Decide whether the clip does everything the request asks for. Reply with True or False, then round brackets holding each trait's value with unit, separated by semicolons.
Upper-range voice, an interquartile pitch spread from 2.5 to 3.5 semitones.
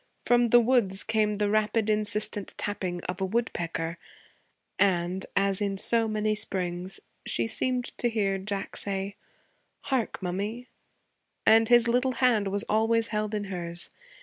True (210 Hz; 2.8 semitones)